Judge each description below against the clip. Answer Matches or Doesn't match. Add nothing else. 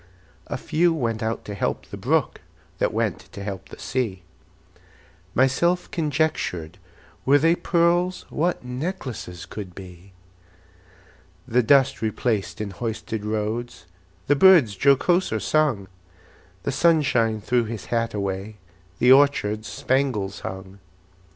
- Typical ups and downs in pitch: Doesn't match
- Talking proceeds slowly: Matches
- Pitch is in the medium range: Doesn't match